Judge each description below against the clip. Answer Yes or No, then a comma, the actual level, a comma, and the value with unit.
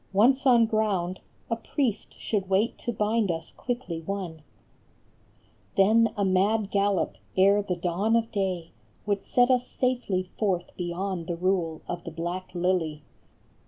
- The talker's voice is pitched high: Yes, high, 195 Hz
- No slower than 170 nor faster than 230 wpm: No, average, 145 wpm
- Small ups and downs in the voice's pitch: No, average, 3.8 semitones